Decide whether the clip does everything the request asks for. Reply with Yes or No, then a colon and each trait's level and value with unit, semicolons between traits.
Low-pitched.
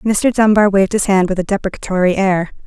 No: high, 195 Hz